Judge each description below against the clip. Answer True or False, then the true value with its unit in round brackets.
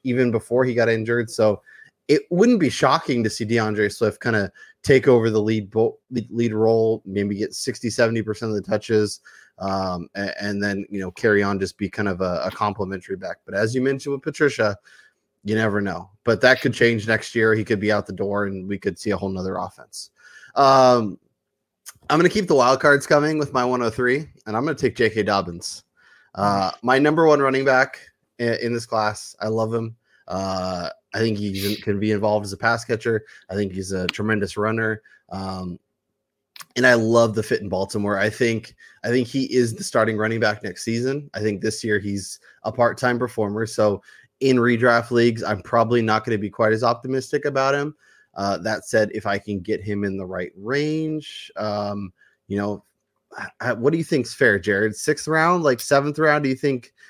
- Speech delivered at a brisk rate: True (210 wpm)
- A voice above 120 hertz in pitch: False (110 Hz)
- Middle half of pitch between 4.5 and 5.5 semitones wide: False (3.5 semitones)